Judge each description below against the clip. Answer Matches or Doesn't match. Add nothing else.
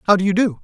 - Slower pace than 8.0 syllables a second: Doesn't match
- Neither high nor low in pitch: Doesn't match